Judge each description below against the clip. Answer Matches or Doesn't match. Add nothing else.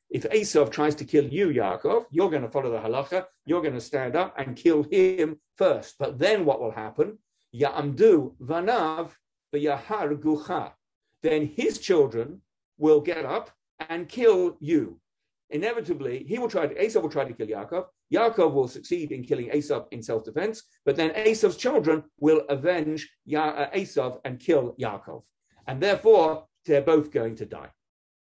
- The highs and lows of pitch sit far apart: Matches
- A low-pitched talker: Doesn't match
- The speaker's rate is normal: Matches